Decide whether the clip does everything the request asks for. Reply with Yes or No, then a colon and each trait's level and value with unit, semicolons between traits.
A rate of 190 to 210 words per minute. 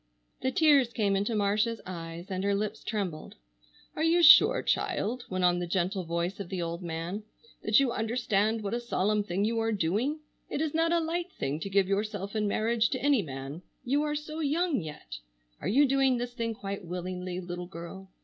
Yes: average, 200 wpm